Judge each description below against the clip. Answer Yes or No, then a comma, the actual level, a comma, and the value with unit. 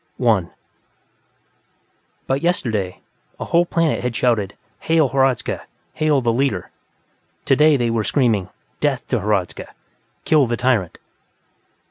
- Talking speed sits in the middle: No, slow, 120 wpm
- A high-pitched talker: No, low, 125 Hz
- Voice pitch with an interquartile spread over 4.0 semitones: Yes, average, 4.8 semitones